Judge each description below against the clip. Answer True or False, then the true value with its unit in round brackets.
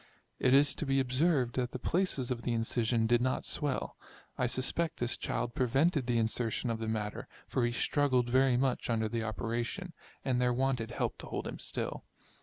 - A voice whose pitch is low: True (125 Hz)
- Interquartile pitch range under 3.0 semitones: True (2.4 semitones)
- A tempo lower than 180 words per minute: False (200 wpm)